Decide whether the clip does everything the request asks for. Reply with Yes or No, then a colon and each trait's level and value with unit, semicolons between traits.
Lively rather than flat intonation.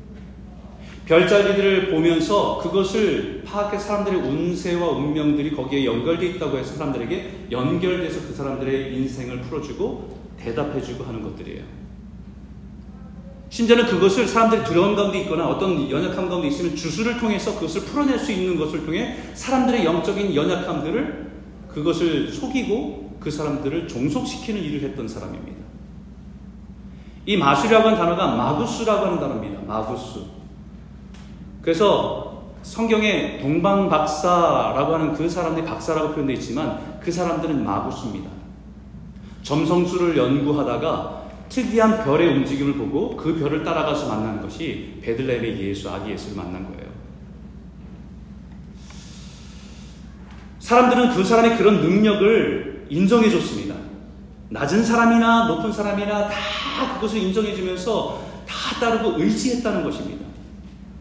Yes: wide, 6.4 semitones